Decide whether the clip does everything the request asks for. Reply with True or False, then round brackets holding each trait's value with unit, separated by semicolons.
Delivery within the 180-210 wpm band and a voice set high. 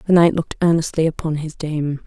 False (205 wpm; 160 Hz)